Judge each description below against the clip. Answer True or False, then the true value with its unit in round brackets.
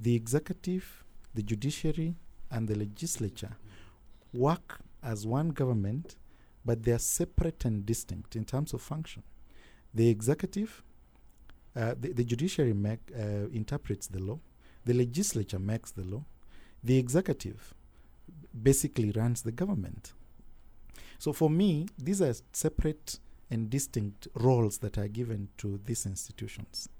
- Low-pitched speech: True (115 Hz)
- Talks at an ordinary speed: False (130 wpm)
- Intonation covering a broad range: True (5.9 semitones)